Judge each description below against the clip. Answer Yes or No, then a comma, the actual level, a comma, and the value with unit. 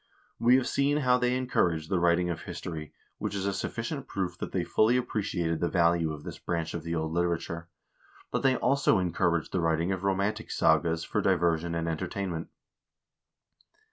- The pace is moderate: Yes, average, 180 wpm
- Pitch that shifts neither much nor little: Yes, average, 3.7 semitones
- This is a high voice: No, very low, 85 Hz